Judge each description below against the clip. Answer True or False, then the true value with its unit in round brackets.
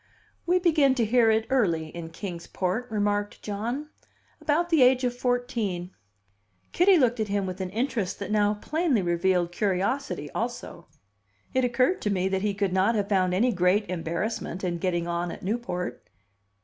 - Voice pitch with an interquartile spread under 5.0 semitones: False (5.3 semitones)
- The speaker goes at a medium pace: True (170 wpm)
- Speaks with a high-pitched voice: True (205 Hz)